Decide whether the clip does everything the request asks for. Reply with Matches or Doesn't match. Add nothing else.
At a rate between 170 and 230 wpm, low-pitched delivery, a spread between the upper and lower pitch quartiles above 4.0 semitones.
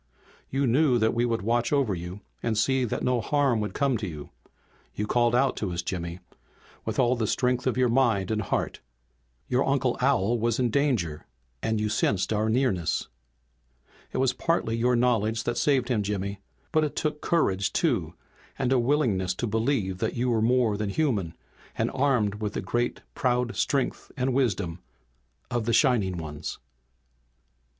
Doesn't match